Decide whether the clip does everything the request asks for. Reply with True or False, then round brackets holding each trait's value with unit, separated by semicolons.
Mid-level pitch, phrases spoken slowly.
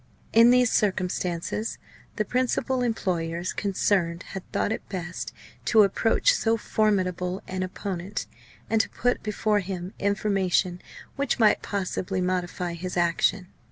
False (195 Hz; 125 wpm)